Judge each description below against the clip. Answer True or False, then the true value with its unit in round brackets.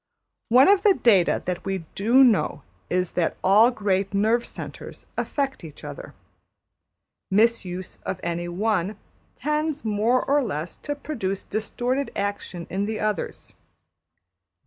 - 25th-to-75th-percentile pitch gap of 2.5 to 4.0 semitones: False (5.1 semitones)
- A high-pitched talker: True (210 Hz)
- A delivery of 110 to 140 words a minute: True (135 wpm)